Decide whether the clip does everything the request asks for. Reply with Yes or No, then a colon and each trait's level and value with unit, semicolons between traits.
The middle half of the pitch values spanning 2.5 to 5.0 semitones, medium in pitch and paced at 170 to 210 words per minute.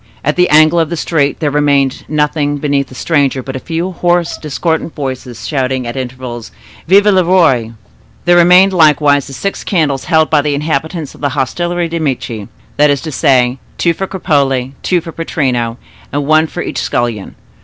Yes: average, 3.9 semitones; medium, 150 Hz; average, 185 wpm